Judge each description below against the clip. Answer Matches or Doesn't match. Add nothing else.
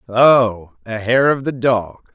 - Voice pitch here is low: Matches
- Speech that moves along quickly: Doesn't match